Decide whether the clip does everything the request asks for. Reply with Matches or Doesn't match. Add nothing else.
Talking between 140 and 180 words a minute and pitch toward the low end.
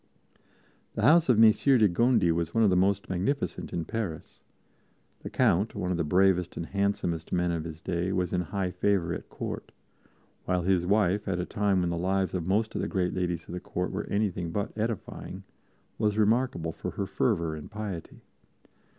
Doesn't match